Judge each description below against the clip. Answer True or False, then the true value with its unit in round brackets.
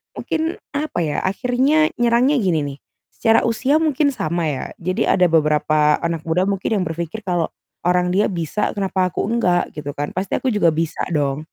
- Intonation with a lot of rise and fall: True (6.4 semitones)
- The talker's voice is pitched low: False (185 Hz)